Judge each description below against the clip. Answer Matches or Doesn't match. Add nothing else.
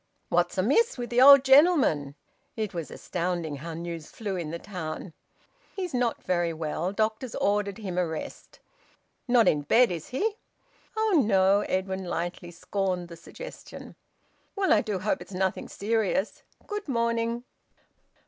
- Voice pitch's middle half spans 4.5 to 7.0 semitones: Matches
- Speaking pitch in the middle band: Doesn't match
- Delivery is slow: Doesn't match